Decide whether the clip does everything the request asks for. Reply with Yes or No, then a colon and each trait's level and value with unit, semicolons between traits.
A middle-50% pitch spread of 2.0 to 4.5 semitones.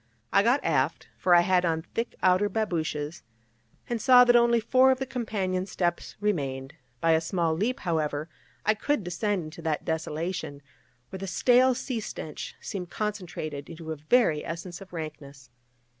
No: average, 5.2 semitones